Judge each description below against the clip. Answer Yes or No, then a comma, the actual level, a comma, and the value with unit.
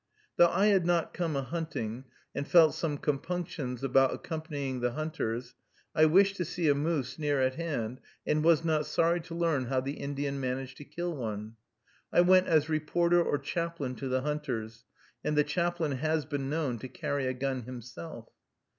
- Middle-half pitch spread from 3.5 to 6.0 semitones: Yes, average, 4.3 semitones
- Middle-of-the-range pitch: Yes, medium, 150 Hz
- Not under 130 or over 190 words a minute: Yes, average, 180 wpm